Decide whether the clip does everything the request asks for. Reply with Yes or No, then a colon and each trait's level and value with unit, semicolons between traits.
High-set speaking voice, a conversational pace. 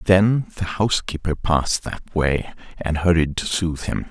No: very low, 85 Hz; average, 160 wpm